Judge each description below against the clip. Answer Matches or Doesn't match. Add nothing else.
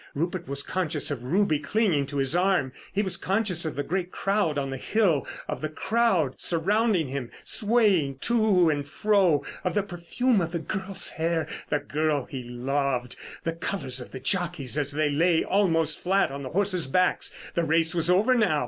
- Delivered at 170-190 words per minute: Matches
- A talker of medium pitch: Matches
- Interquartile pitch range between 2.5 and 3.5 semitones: Doesn't match